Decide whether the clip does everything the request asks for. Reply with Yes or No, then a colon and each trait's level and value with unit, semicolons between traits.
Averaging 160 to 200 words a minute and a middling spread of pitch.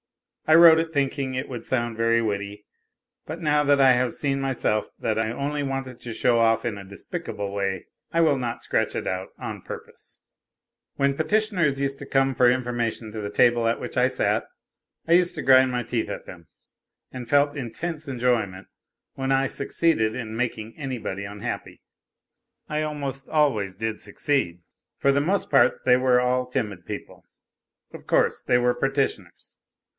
Yes: average, 180 wpm; average, 3.9 semitones